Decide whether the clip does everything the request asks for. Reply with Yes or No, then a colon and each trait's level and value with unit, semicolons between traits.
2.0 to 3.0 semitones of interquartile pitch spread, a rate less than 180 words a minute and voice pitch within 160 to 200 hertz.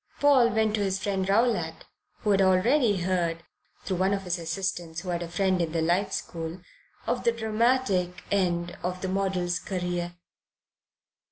Yes: average, 2.7 semitones; average, 165 wpm; medium, 185 Hz